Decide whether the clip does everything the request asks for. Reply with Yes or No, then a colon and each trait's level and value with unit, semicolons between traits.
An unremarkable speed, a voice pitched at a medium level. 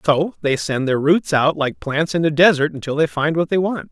No: fast, 260 wpm; medium, 150 Hz